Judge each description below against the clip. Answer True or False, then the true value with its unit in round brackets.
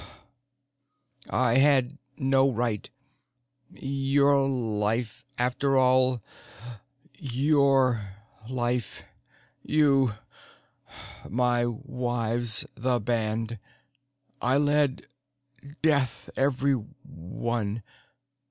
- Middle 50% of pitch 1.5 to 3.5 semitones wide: True (2.7 semitones)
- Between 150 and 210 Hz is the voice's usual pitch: False (125 Hz)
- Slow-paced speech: True (60 wpm)